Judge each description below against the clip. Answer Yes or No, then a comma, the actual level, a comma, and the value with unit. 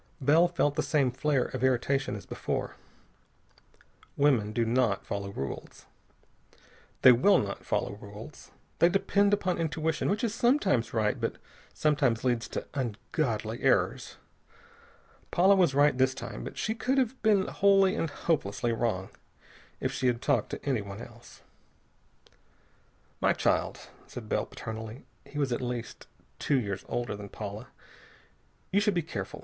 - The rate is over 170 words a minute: No, average, 145 wpm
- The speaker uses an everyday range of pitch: No, wide, 7.3 semitones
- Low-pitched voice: Yes, low, 130 Hz